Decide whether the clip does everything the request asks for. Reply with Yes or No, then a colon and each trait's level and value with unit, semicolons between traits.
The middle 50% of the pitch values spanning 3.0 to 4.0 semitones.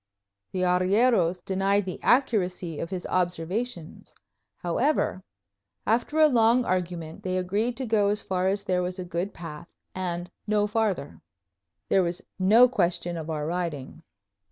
Yes: average, 3.3 semitones